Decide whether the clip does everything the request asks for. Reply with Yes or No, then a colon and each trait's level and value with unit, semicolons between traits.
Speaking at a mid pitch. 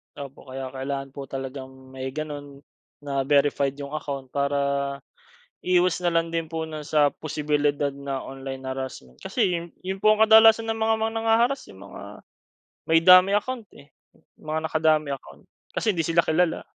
Yes: medium, 145 Hz